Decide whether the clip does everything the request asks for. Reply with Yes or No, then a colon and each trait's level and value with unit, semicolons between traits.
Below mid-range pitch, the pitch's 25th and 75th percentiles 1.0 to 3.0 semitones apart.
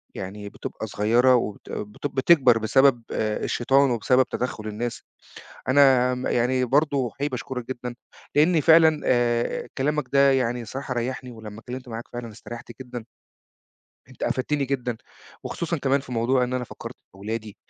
Yes: low, 125 Hz; narrow, 2.5 semitones